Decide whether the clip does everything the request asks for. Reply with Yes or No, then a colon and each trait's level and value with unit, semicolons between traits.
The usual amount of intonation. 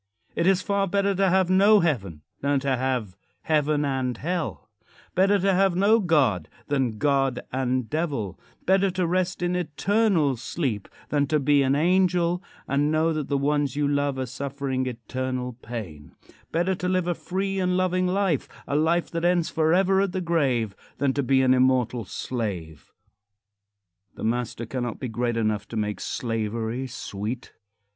No: wide, 6.3 semitones